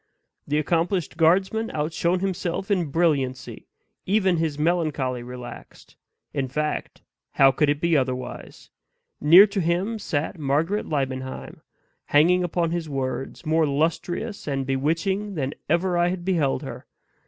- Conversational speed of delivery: No, slow, 130 wpm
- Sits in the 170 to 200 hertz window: No, medium, 160 Hz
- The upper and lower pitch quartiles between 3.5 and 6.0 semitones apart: Yes, average, 4.2 semitones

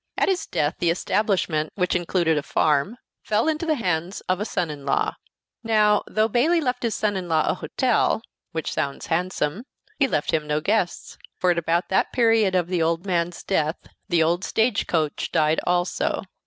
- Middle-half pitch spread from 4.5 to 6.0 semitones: Yes, average, 5.1 semitones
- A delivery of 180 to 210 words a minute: Yes, average, 190 wpm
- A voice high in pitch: No, medium, 180 Hz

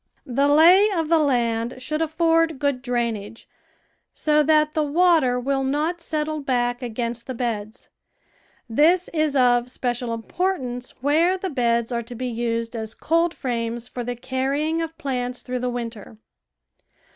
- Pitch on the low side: No, very high, 260 Hz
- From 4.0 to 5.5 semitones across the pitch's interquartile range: Yes, average, 4.4 semitones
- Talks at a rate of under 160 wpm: Yes, average, 150 wpm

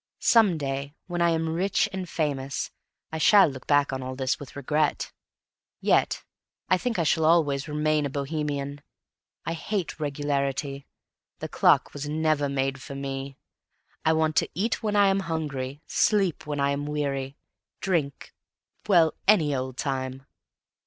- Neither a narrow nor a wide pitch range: Yes, average, 3.0 semitones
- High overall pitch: No, medium, 150 Hz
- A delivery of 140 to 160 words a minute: Yes, average, 155 wpm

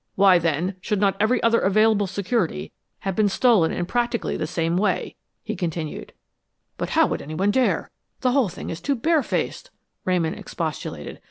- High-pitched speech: Yes, high, 195 Hz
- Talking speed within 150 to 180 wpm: Yes, average, 170 wpm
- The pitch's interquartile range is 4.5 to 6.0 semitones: Yes, average, 4.9 semitones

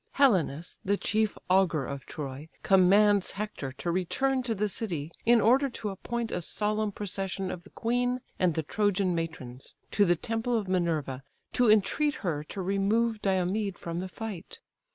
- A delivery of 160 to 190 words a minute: Yes, average, 165 wpm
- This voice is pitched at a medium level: No, high, 195 Hz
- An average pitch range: Yes, average, 4.2 semitones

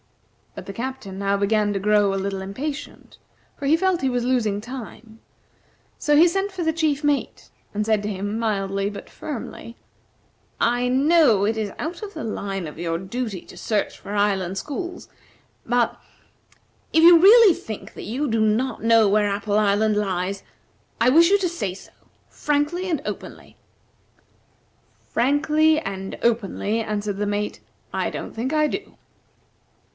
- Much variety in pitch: Yes, wide, 6.5 semitones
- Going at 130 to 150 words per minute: No, average, 160 wpm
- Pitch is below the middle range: No, high, 225 Hz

